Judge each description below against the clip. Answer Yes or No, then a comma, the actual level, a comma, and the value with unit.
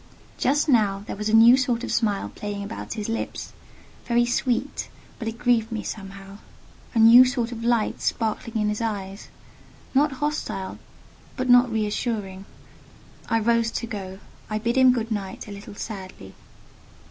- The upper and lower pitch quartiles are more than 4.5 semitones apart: No, average, 2.7 semitones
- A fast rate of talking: No, average, 150 wpm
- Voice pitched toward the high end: Yes, high, 225 Hz